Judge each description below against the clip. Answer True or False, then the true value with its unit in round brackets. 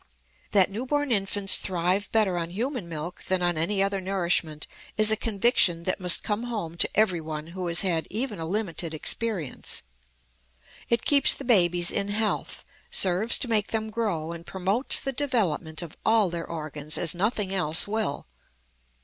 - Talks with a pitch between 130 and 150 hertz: False (190 Hz)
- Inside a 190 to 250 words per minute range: False (165 wpm)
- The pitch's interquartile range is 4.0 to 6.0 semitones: True (4.3 semitones)